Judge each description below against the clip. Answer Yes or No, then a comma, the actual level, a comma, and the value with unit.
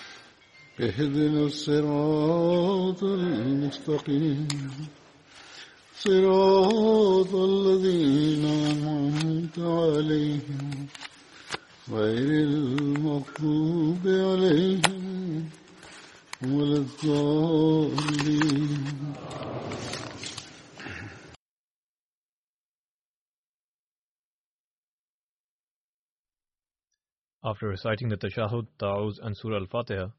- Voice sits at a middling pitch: Yes, medium, 150 Hz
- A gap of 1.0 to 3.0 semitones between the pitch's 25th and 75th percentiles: Yes, narrow, 2.5 semitones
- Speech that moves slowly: Yes, slow, 40 wpm